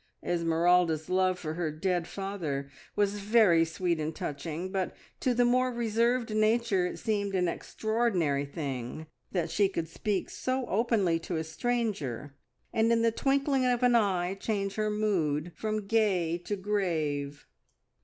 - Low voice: No, high, 190 Hz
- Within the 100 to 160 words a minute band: Yes, average, 150 wpm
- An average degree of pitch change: Yes, average, 5.0 semitones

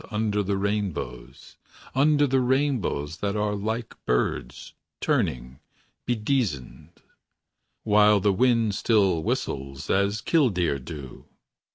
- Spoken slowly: Yes, slow, 100 wpm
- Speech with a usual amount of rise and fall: No, wide, 6.5 semitones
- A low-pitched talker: Yes, low, 105 Hz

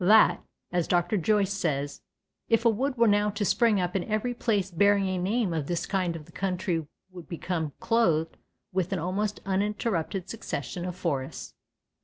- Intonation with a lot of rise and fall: No, average, 3.4 semitones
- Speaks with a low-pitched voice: No, high, 190 Hz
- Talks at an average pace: Yes, average, 170 wpm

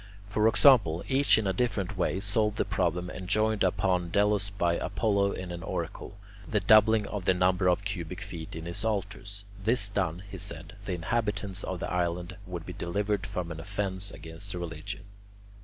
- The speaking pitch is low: Yes, very low, 95 Hz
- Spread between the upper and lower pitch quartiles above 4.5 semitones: No, average, 2.7 semitones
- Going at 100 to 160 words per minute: No, average, 175 wpm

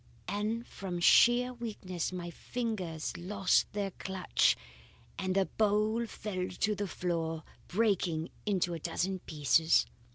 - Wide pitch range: No, average, 3.4 semitones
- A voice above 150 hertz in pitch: Yes, high, 190 Hz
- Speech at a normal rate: No, slow, 125 wpm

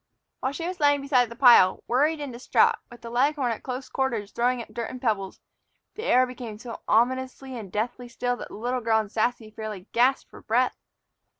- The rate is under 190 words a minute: No, fast, 205 wpm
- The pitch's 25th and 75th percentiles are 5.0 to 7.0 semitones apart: No, narrow, 2.5 semitones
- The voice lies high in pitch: Yes, high, 245 Hz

